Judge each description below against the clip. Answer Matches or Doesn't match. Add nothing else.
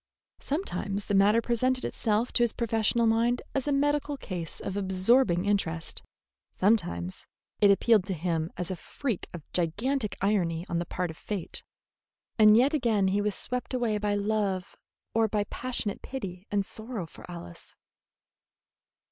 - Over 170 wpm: Doesn't match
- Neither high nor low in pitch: Doesn't match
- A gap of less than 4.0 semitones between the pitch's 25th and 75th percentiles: Doesn't match